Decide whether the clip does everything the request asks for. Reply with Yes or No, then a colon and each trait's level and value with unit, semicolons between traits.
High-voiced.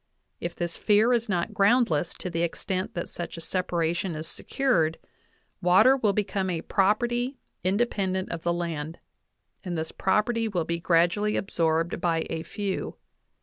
No: medium, 180 Hz